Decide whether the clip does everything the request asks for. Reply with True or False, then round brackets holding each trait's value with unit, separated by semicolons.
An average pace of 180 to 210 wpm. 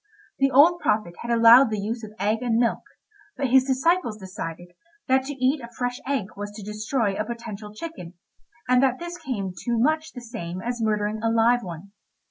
True (195 wpm)